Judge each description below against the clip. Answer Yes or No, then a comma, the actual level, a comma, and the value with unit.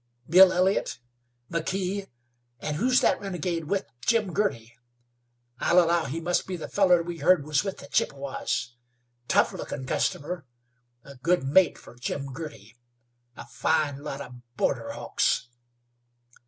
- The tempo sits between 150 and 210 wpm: No, average, 140 wpm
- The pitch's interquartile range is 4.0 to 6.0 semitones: Yes, average, 4.9 semitones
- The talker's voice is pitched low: No, medium, 165 Hz